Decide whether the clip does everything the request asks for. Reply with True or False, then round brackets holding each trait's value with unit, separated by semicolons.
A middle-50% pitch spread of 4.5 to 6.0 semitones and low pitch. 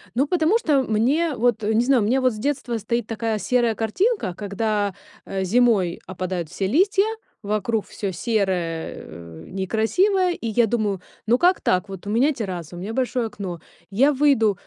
False (5.0 semitones; 220 Hz)